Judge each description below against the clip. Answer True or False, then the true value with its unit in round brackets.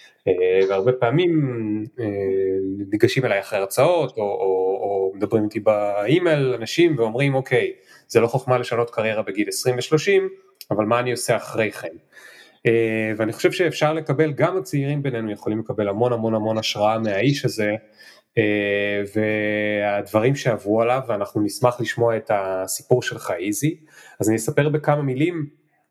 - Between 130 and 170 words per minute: True (145 wpm)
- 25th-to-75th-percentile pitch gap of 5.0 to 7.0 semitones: True (5.5 semitones)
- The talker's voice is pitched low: True (115 Hz)